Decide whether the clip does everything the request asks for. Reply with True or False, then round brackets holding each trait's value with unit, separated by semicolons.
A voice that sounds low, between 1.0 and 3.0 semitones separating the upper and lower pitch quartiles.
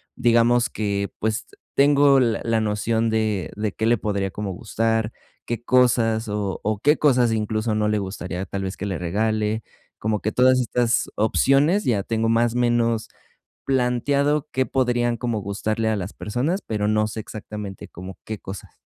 True (110 Hz; 2.5 semitones)